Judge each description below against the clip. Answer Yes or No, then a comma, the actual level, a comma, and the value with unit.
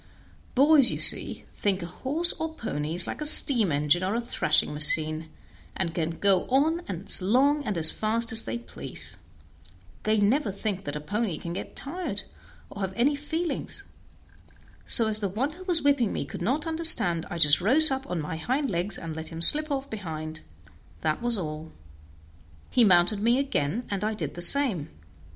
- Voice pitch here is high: Yes, high, 210 Hz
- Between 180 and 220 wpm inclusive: Yes, average, 185 wpm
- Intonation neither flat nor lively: No, wide, 8.3 semitones